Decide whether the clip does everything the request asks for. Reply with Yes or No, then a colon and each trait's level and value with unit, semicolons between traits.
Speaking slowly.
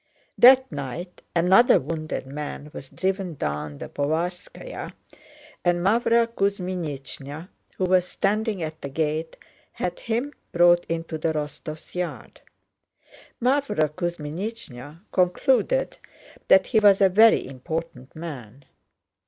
Yes: slow, 110 wpm